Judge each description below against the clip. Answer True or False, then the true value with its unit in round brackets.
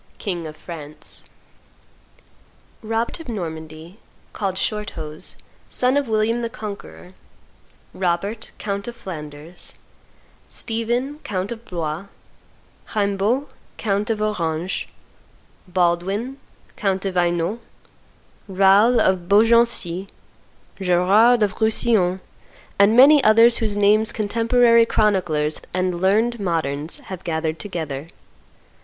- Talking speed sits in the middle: False (100 wpm)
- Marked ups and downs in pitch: False (4.6 semitones)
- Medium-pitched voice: False (200 Hz)